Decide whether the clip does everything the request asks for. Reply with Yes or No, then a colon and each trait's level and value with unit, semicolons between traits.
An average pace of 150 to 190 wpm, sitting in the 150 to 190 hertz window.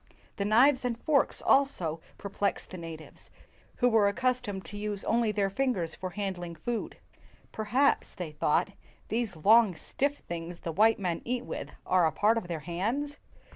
No: average, 175 wpm; high, 205 Hz